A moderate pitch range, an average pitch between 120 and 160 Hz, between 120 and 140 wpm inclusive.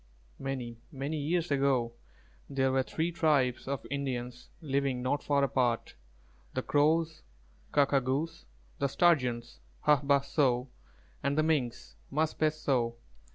Yes: average, 3.1 semitones; medium, 140 Hz; slow, 135 wpm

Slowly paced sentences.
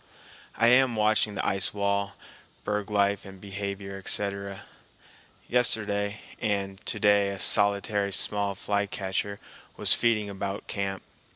Yes: slow, 120 wpm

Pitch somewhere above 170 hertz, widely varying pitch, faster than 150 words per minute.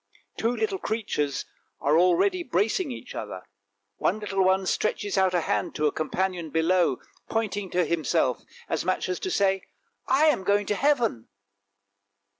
No: high, 190 Hz; average, 4.9 semitones; average, 160 wpm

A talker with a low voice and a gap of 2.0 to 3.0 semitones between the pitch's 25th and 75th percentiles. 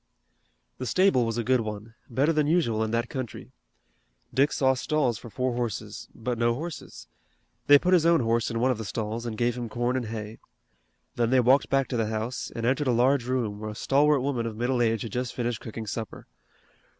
Yes: low, 120 Hz; narrow, 2.6 semitones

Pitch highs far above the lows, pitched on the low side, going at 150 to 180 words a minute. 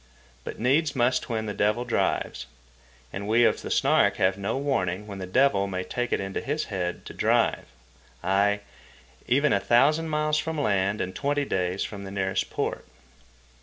Yes: wide, 6.1 semitones; low, 105 Hz; average, 175 wpm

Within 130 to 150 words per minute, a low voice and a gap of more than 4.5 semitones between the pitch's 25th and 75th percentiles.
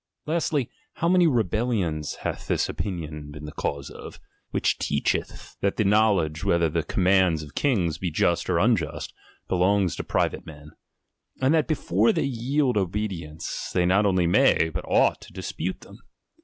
No: average, 165 wpm; very low, 95 Hz; wide, 5.6 semitones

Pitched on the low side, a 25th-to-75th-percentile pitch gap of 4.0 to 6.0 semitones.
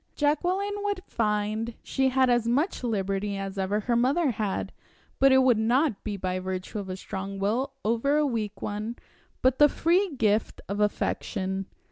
No: high, 225 Hz; average, 5.1 semitones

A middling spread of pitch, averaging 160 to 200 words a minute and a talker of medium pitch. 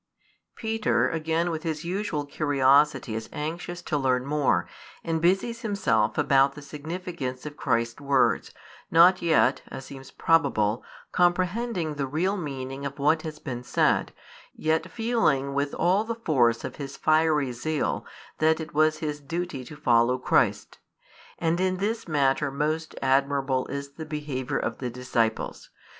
No: average, 3.8 semitones; average, 150 wpm; medium, 150 Hz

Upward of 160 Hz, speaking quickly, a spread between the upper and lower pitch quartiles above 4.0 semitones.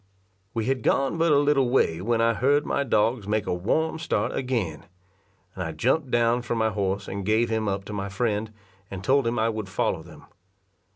No: low, 115 Hz; fast, 210 wpm; average, 4.6 semitones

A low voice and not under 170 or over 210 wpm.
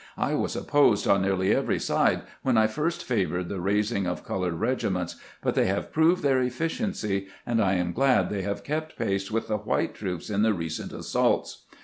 Yes: low, 105 Hz; average, 195 wpm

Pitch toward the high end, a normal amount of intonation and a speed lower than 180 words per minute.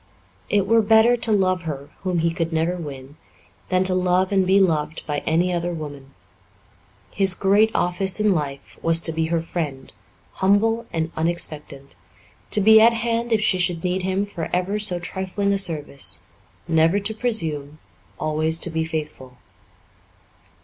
No: medium, 180 Hz; average, 3.8 semitones; average, 165 wpm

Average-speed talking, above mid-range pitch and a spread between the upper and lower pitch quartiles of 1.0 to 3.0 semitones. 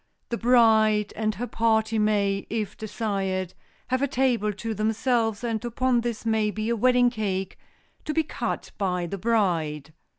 Yes: average, 160 wpm; high, 220 Hz; narrow, 2.6 semitones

